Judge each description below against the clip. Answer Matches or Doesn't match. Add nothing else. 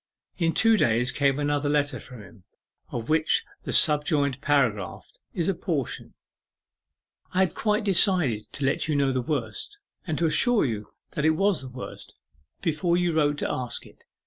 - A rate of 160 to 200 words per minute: Matches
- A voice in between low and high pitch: Matches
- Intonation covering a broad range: Doesn't match